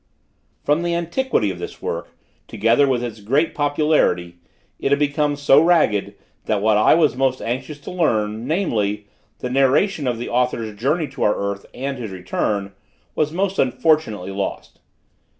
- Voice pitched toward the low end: Yes, low, 130 Hz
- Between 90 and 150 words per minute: No, average, 160 wpm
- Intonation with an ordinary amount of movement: No, wide, 6.2 semitones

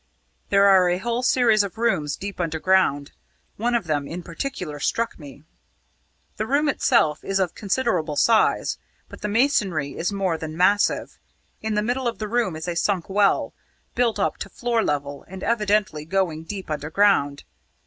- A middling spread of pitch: No, wide, 5.7 semitones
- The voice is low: No, high, 195 Hz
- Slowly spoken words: No, average, 170 wpm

